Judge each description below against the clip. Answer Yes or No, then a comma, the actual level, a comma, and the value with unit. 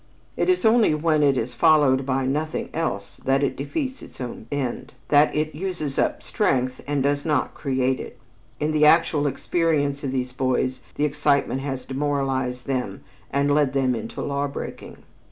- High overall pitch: No, medium, 140 Hz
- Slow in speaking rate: No, average, 170 wpm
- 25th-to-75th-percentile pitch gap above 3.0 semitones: No, narrow, 2.5 semitones